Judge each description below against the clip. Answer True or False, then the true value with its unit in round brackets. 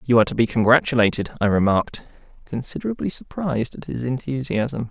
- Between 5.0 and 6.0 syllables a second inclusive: False (6.2 syllables/s)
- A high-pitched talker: False (125 Hz)